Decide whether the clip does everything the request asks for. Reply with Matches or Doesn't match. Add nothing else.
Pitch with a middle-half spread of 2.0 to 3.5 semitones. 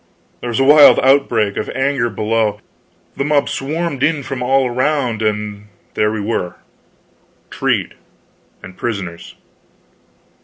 Doesn't match